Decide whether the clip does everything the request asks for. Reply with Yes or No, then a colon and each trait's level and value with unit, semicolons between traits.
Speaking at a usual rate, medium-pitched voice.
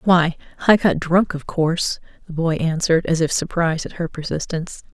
Yes: average, 180 wpm; medium, 165 Hz